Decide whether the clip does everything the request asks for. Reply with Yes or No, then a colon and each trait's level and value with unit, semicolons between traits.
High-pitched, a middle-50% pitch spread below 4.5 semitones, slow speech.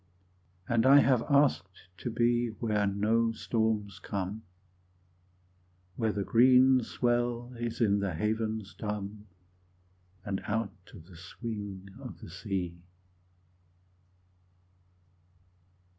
No: low, 110 Hz; average, 3.0 semitones; slow, 100 wpm